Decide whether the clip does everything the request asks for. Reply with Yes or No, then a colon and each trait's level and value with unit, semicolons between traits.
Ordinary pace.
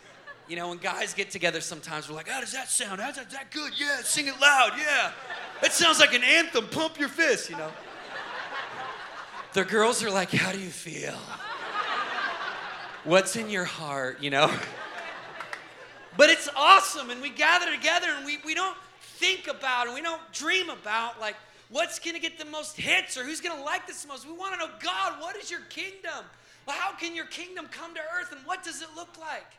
No: fast, 215 wpm